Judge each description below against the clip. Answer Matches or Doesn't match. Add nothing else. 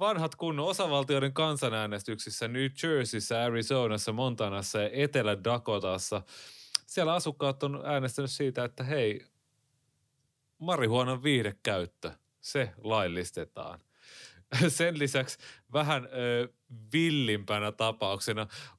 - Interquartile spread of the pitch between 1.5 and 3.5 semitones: Doesn't match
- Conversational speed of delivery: Doesn't match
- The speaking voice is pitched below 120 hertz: Doesn't match